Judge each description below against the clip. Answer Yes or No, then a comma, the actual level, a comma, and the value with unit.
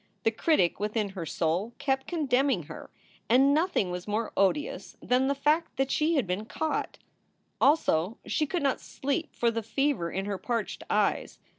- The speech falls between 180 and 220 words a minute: No, average, 170 wpm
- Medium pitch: No, very high, 250 Hz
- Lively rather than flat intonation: Yes, wide, 6.3 semitones